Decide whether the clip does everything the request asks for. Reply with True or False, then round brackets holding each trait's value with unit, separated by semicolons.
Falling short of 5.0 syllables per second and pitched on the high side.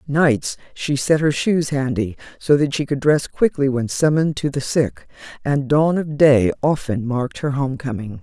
False (4.6 syllables/s; 140 Hz)